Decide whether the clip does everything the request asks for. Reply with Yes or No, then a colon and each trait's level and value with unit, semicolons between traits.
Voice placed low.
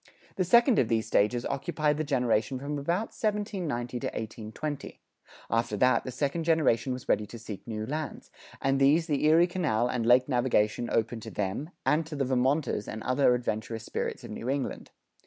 Yes: low, 130 Hz